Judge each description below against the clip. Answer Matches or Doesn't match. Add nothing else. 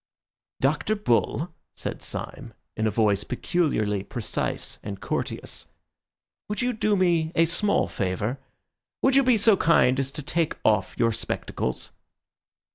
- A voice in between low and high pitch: Matches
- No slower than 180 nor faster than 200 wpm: Doesn't match